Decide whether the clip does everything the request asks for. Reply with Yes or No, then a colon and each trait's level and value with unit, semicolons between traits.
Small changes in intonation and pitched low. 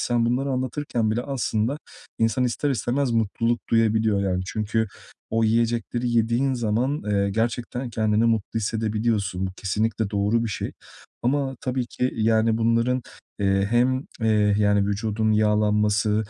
Yes: narrow, 2.2 semitones; low, 115 Hz